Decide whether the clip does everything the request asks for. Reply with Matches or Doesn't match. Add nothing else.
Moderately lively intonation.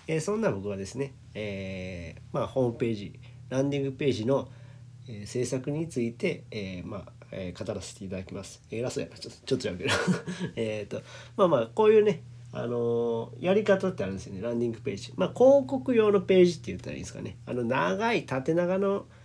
Doesn't match